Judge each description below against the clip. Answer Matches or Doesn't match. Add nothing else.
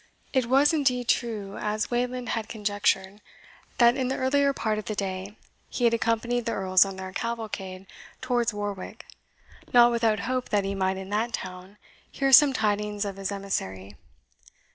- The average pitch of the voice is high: Matches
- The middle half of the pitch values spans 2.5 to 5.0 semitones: Matches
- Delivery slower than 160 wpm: Doesn't match